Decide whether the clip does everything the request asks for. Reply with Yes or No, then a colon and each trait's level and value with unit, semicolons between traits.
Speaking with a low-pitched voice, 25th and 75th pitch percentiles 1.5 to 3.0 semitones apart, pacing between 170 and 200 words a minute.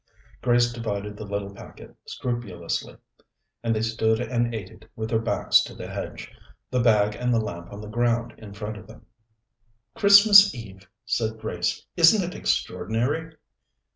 No: low, 110 Hz; average, 2.7 semitones; average, 160 wpm